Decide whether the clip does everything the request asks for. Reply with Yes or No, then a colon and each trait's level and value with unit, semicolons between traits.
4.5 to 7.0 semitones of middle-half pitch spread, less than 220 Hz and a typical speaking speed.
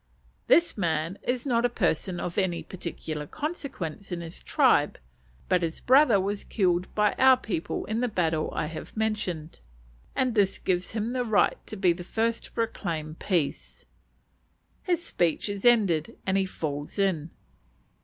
Yes: average, 5.3 semitones; high, 190 Hz; average, 160 wpm